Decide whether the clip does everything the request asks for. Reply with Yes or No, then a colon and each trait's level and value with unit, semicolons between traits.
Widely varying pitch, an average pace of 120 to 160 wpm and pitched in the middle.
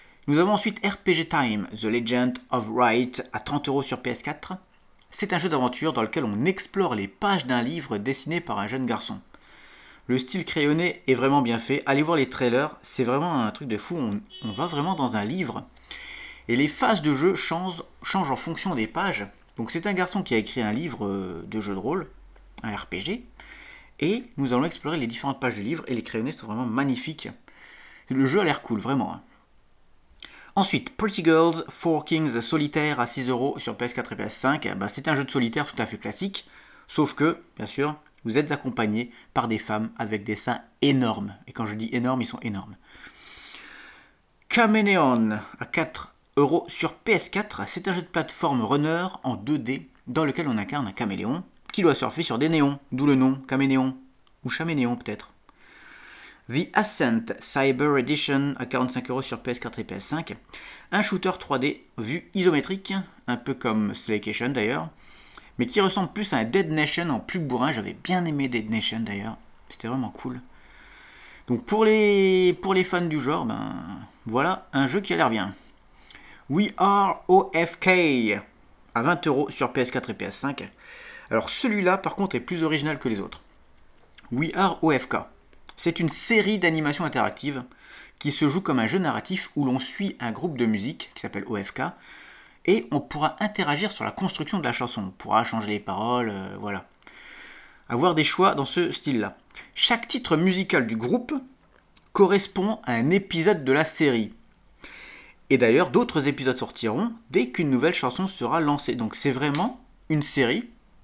No: wide, 6.8 semitones; average, 175 wpm; medium, 145 Hz